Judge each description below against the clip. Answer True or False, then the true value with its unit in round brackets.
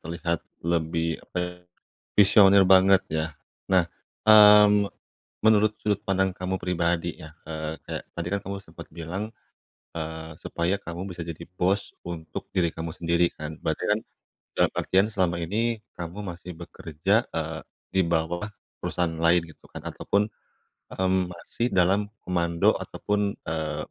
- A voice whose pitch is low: True (90 Hz)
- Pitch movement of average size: True (3.0 semitones)